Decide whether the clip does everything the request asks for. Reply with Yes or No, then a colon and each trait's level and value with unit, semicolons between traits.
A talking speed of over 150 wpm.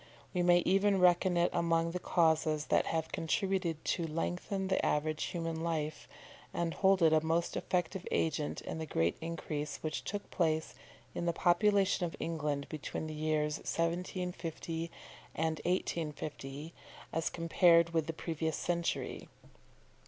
No: average, 145 wpm